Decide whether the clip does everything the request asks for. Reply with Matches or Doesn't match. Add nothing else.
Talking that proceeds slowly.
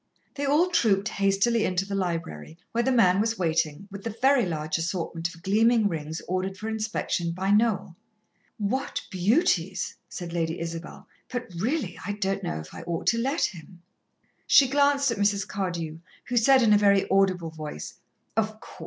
Doesn't match